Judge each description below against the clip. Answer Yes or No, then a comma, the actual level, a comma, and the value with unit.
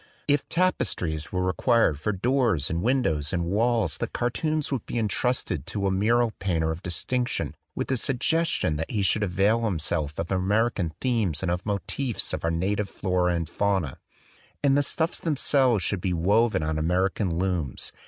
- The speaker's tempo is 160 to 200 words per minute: Yes, average, 175 wpm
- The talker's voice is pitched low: Yes, low, 100 Hz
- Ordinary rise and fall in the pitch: No, wide, 5.9 semitones